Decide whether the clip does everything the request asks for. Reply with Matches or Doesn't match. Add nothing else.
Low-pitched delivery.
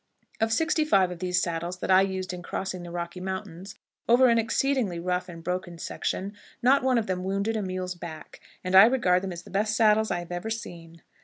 Doesn't match